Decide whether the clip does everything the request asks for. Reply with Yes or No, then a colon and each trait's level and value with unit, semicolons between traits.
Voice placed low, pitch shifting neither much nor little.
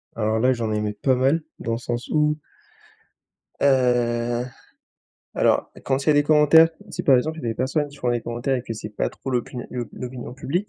Yes: low, 125 Hz; average, 3.4 semitones